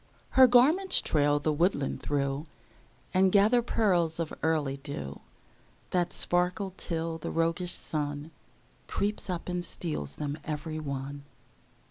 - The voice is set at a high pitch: No, medium, 165 Hz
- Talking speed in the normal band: No, slow, 125 wpm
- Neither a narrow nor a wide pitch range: Yes, average, 4.0 semitones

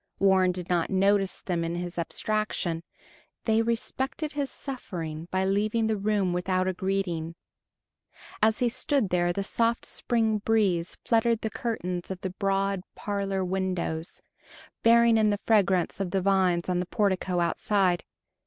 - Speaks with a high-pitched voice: Yes, high, 195 Hz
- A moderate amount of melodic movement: Yes, average, 3.4 semitones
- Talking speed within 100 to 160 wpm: Yes, average, 150 wpm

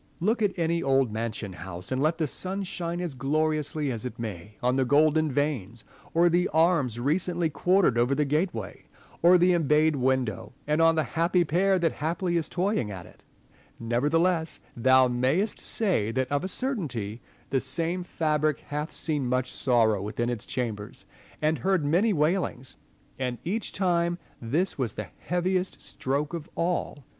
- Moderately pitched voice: Yes, medium, 150 Hz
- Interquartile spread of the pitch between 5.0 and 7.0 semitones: Yes, wide, 5.5 semitones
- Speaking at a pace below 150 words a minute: No, average, 165 wpm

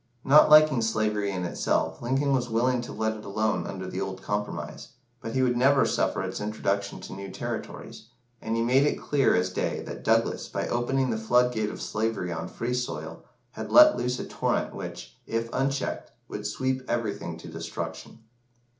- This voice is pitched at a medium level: No, low, 115 Hz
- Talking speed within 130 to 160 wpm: No, average, 185 wpm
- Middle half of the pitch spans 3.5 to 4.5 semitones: Yes, average, 4.0 semitones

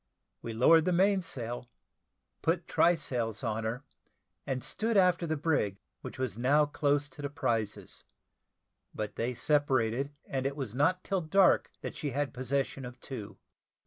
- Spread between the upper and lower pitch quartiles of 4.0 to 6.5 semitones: Yes, average, 4.7 semitones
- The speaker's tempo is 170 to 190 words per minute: No, average, 155 wpm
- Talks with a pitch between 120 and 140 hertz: Yes, low, 135 Hz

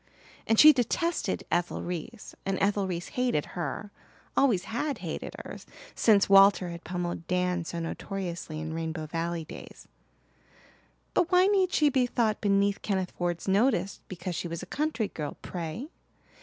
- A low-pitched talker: No, high, 195 Hz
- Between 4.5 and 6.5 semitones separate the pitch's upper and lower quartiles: Yes, wide, 5.4 semitones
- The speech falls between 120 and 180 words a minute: Yes, average, 155 wpm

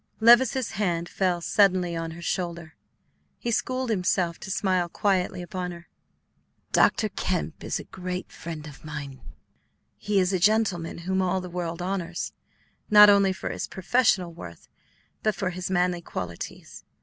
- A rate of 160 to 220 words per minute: No, average, 150 wpm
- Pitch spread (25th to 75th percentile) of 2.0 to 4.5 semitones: Yes, narrow, 2.5 semitones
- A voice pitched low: No, medium, 180 Hz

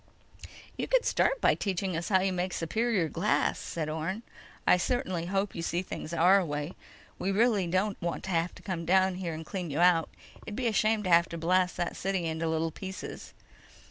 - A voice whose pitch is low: No, medium, 180 Hz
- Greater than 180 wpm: Yes, fast, 205 wpm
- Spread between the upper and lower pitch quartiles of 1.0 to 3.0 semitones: Yes, average, 2.7 semitones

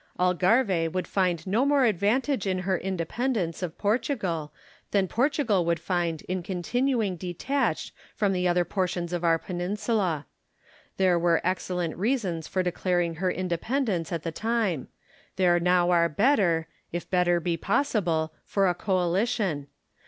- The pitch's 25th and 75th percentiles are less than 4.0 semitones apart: Yes, average, 3.4 semitones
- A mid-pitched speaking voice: Yes, medium, 180 Hz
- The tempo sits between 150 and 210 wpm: No, average, 140 wpm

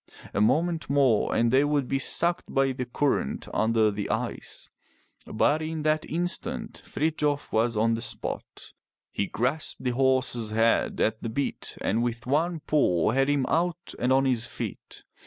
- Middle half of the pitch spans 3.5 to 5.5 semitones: Yes, average, 4.6 semitones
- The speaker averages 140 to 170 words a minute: Yes, average, 165 wpm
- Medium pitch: No, low, 130 Hz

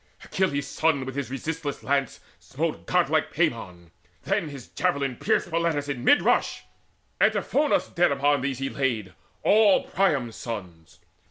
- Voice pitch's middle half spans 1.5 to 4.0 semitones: No, average, 4.5 semitones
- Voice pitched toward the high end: No, medium, 140 Hz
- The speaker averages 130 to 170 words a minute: Yes, average, 140 wpm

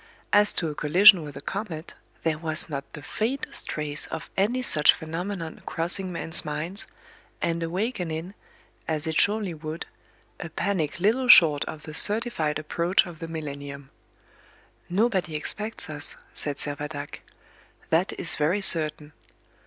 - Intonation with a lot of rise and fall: No, average, 4.2 semitones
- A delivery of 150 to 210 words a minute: No, average, 140 wpm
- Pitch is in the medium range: Yes, medium, 165 Hz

